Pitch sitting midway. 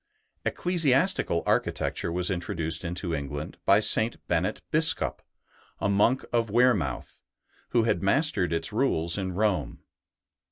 No: low, 100 Hz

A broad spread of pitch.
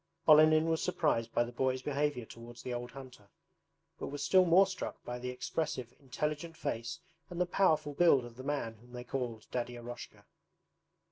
No: average, 4.3 semitones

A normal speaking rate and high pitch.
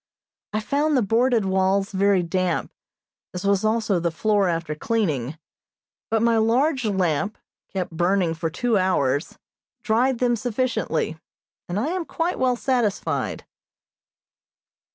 No: slow, 130 wpm; high, 205 Hz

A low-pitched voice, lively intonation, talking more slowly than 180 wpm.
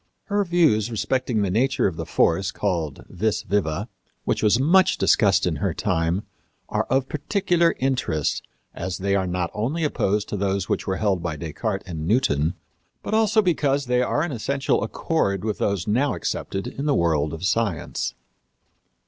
Yes: low, 105 Hz; wide, 6.8 semitones; average, 170 wpm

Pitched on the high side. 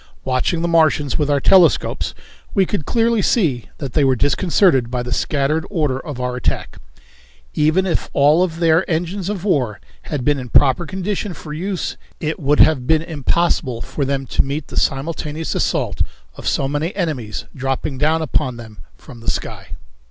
No: medium, 150 Hz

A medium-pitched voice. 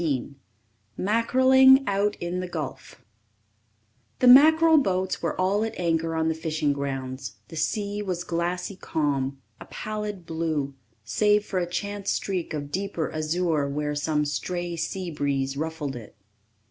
Yes: medium, 170 Hz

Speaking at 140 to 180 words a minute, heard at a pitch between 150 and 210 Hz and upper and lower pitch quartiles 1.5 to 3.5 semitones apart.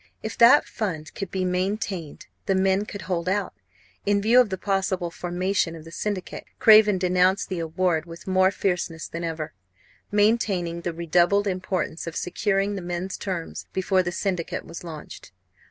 Yes: average, 165 wpm; medium, 185 Hz; narrow, 2.6 semitones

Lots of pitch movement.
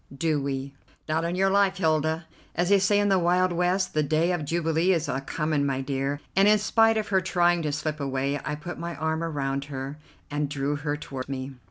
No: average, 3.9 semitones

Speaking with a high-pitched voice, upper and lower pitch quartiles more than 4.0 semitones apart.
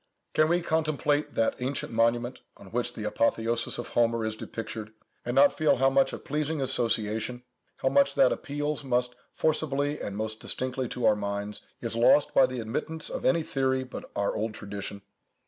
No: low, 125 Hz; average, 4.5 semitones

